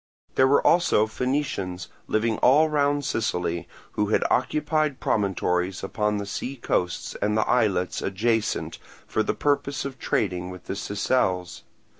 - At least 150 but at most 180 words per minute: No, average, 140 wpm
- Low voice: Yes, low, 110 Hz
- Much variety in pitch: Yes, wide, 6.1 semitones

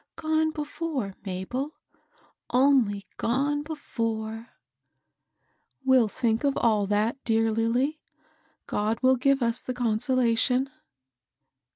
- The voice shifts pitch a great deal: No, average, 3.7 semitones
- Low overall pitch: No, high, 245 Hz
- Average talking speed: No, slow, 110 wpm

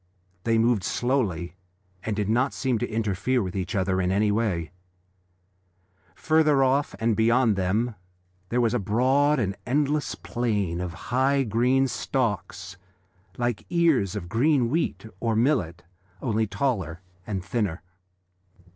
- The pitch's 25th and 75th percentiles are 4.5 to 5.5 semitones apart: Yes, average, 4.9 semitones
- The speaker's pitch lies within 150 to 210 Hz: No, low, 115 Hz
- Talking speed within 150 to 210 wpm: No, slow, 135 wpm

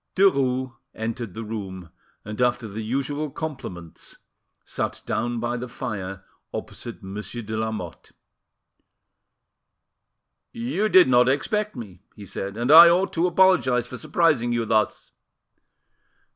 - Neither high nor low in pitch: No, low, 120 Hz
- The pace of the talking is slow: Yes, slow, 125 wpm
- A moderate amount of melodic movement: Yes, average, 4.8 semitones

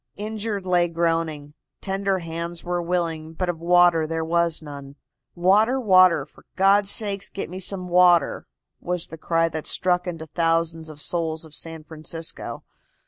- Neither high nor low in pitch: Yes, medium, 170 Hz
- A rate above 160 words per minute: No, average, 155 wpm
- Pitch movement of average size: No, narrow, 2.2 semitones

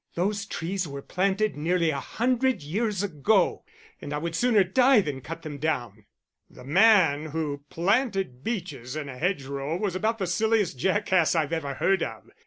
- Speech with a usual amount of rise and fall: No, wide, 5.8 semitones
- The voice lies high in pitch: No, medium, 175 Hz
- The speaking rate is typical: Yes, average, 170 wpm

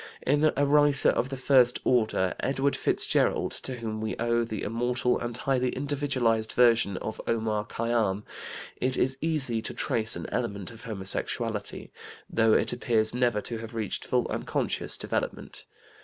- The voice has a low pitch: Yes, low, 120 Hz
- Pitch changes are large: No, average, 2.8 semitones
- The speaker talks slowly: No, average, 155 wpm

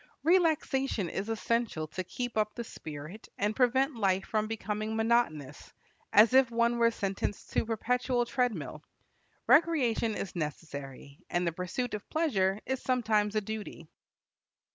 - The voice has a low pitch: No, high, 220 Hz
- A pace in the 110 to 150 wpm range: Yes, average, 140 wpm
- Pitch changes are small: No, average, 4.6 semitones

